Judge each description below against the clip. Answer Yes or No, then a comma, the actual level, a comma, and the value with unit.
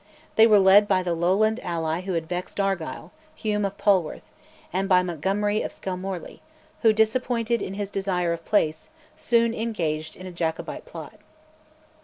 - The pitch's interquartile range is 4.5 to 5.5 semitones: No, average, 3.5 semitones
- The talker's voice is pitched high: Yes, high, 195 Hz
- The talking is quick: No, average, 160 wpm